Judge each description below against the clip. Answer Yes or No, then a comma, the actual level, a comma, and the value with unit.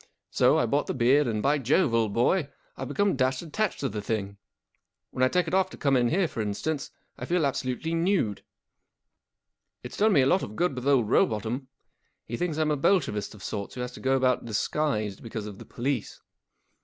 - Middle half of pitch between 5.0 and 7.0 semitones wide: Yes, wide, 5.5 semitones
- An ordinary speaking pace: No, fast, 210 wpm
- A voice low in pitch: Yes, low, 130 Hz